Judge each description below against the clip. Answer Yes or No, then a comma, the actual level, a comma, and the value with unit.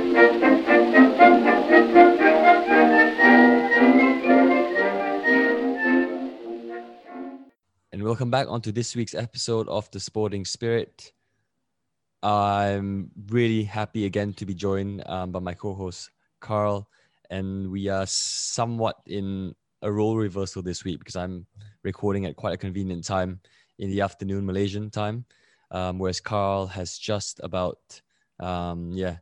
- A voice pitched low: Yes, low, 100 Hz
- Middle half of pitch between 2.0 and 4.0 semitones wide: Yes, average, 3.2 semitones